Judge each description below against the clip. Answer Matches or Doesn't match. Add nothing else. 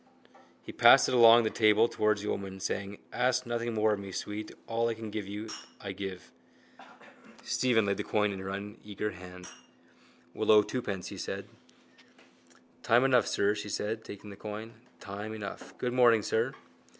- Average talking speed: Matches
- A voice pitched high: Doesn't match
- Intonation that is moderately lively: Doesn't match